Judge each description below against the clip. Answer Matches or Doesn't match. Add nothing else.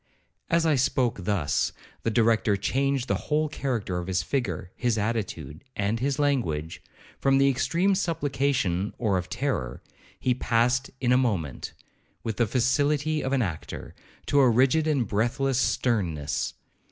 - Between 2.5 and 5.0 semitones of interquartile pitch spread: Doesn't match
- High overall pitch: Doesn't match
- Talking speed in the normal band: Matches